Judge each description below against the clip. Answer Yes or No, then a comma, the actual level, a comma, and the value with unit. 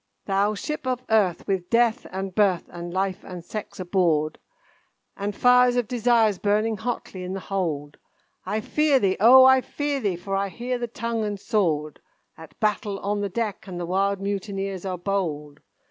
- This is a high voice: Yes, high, 200 Hz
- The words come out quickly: No, average, 175 wpm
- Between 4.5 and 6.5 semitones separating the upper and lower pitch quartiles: No, average, 3.6 semitones